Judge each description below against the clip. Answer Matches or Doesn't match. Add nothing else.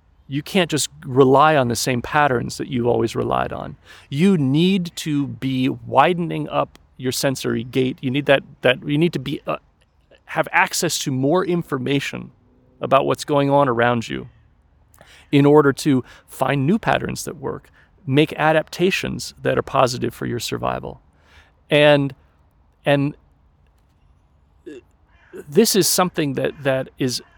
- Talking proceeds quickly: Doesn't match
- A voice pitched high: Doesn't match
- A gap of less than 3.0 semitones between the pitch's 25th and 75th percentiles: Doesn't match